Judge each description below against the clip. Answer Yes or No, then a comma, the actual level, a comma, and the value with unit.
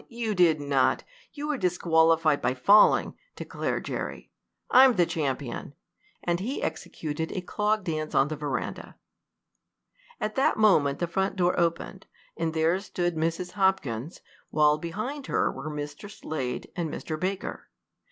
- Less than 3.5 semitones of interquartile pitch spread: No, average, 4.1 semitones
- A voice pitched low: No, medium, 170 Hz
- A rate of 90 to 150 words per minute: Yes, average, 140 wpm